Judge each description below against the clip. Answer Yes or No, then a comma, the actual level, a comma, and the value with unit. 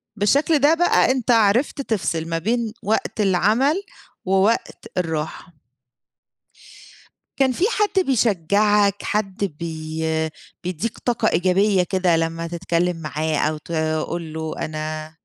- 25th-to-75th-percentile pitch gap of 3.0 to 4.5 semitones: No, wide, 5.5 semitones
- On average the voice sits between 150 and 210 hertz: Yes, high, 190 Hz